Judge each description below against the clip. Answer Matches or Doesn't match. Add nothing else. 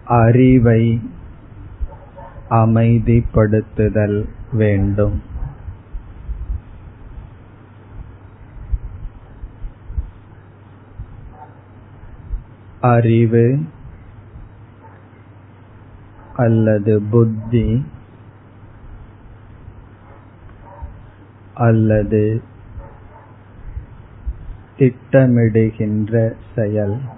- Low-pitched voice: Matches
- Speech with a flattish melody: Matches